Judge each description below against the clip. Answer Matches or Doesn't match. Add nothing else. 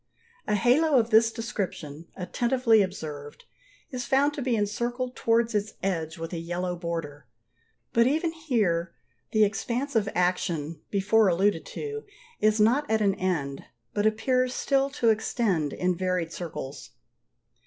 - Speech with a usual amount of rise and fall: Doesn't match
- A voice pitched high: Matches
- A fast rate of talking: Doesn't match